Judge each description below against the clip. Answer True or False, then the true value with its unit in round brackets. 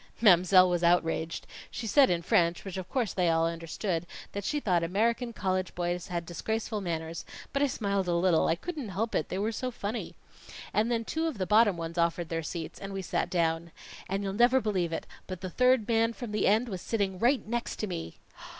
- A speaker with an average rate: False (215 wpm)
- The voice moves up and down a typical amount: True (4.7 semitones)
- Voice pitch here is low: False (190 Hz)